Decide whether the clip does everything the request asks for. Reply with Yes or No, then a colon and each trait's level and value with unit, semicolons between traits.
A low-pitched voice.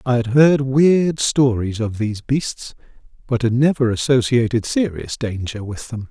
Yes: low, 125 Hz